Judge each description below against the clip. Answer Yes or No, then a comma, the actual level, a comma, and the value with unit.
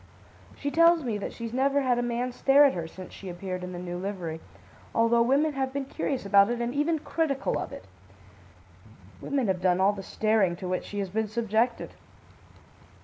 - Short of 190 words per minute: No, average, 200 wpm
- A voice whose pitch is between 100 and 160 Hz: No, high, 230 Hz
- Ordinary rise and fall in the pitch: No, wide, 6.1 semitones